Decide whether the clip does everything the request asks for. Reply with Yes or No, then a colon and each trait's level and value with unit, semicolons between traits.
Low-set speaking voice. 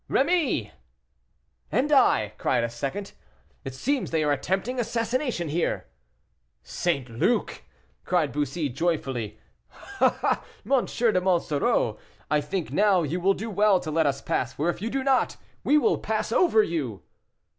No: medium, 175 Hz